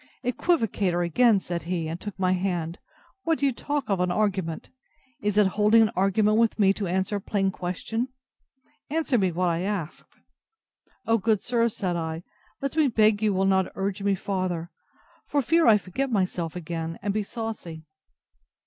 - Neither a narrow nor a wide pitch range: Yes, average, 3.8 semitones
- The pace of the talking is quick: No, average, 175 wpm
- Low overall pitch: No, high, 195 Hz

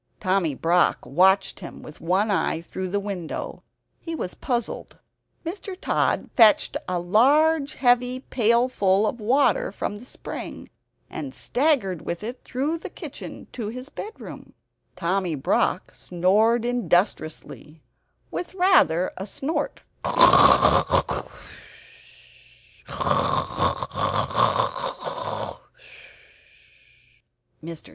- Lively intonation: Yes, wide, 6.2 semitones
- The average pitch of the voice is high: Yes, high, 215 Hz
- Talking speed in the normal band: No, slow, 90 wpm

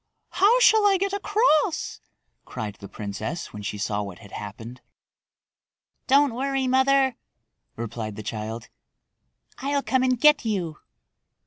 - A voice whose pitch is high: Yes, high, 240 Hz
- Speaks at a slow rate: Yes, slow, 130 wpm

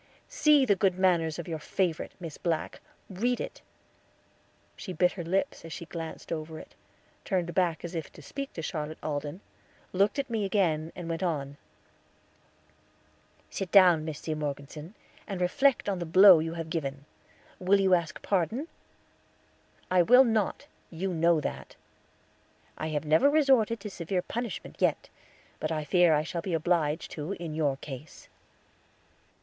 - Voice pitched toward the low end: No, medium, 170 Hz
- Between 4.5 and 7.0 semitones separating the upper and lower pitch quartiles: No, average, 3.6 semitones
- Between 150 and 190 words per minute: Yes, average, 160 wpm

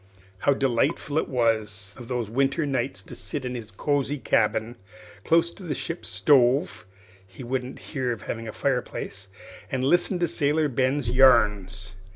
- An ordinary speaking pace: Yes, average, 155 wpm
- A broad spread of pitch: No, average, 4.1 semitones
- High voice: No, low, 130 Hz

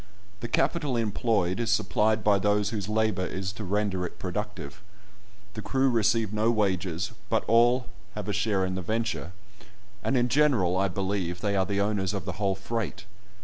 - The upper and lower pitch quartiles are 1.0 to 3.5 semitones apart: Yes, average, 2.9 semitones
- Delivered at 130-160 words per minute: No, average, 180 wpm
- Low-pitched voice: Yes, low, 105 Hz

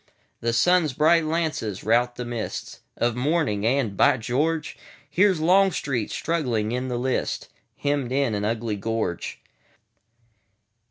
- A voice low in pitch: Yes, low, 125 Hz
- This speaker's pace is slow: Yes, slow, 110 wpm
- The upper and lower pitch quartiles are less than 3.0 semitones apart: No, wide, 5.4 semitones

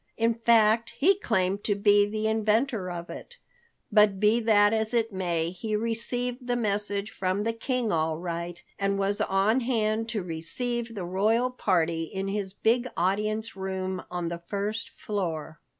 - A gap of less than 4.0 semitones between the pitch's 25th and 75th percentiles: Yes, average, 3.4 semitones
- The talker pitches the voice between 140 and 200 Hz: No, high, 210 Hz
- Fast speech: No, average, 165 wpm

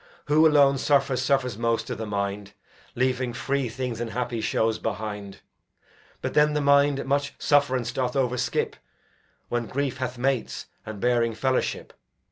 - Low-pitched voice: Yes, low, 125 Hz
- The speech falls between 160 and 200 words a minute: No, average, 145 wpm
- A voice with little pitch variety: No, average, 3.4 semitones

